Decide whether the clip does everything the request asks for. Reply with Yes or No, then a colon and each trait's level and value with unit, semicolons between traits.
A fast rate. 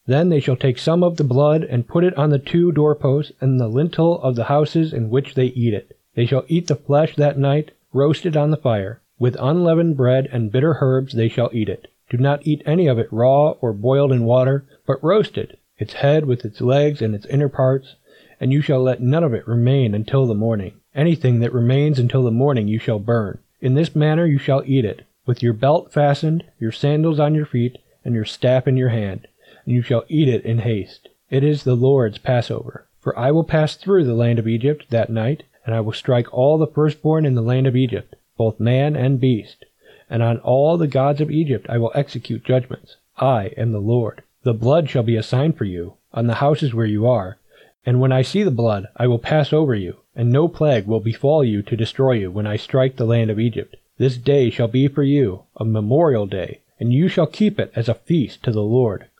Yes: fast, 230 wpm